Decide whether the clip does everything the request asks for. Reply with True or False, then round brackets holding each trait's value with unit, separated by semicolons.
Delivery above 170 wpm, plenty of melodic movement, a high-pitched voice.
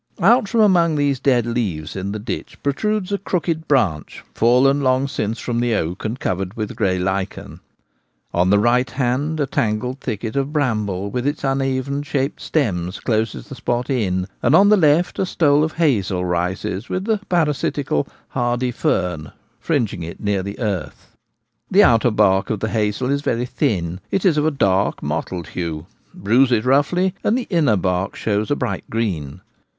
False (180 wpm; 6.6 semitones; 120 Hz)